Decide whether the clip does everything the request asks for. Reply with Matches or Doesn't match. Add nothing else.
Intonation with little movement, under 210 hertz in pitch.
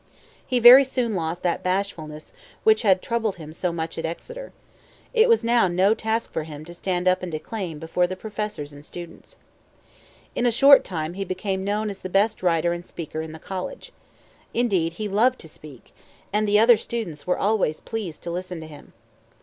Doesn't match